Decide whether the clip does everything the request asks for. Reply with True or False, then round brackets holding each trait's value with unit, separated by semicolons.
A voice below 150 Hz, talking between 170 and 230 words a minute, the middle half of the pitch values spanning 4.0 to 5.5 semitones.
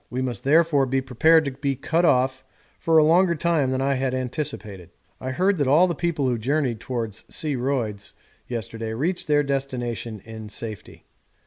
True (135 Hz; 175 wpm; 4.3 semitones)